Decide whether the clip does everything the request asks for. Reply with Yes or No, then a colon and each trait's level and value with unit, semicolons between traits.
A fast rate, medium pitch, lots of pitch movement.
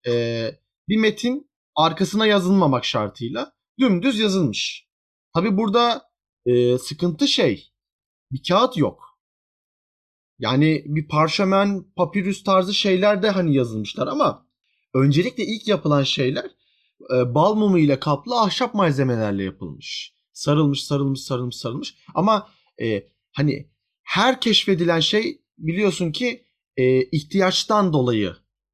No: average, 110 wpm; medium, 165 Hz; wide, 7.6 semitones